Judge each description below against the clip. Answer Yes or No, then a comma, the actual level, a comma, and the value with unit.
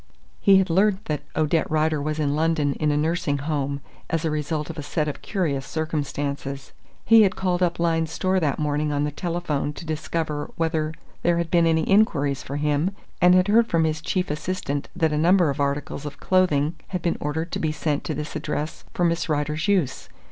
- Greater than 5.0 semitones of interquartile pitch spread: No, average, 2.8 semitones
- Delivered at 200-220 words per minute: Yes, fast, 205 wpm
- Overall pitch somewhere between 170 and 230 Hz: No, medium, 155 Hz